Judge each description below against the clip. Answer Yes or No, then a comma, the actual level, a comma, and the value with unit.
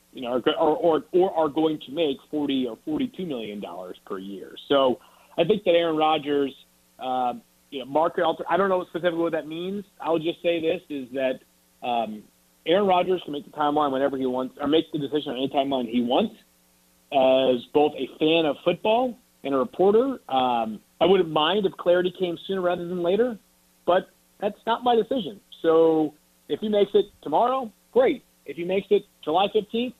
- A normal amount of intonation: No, wide, 6.5 semitones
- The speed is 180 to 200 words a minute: Yes, average, 190 wpm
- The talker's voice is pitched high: No, medium, 160 Hz